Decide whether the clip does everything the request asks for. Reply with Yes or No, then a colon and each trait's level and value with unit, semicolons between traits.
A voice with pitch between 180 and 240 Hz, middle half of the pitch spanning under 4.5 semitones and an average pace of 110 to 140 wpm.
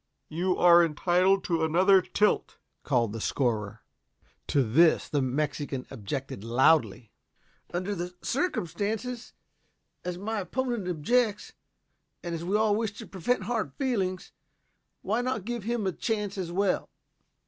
No: medium, 185 Hz; wide, 5.4 semitones; slow, 135 wpm